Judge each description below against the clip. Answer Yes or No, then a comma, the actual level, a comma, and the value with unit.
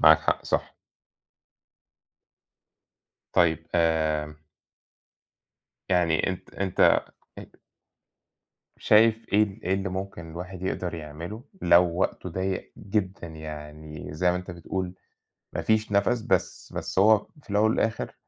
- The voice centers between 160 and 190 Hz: No, very low, 90 Hz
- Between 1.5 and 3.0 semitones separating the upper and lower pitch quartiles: No, average, 3.7 semitones